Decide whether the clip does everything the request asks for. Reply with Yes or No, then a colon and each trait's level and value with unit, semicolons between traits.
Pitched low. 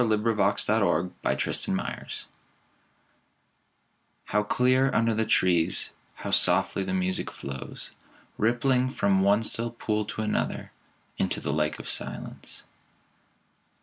Yes: low, 105 Hz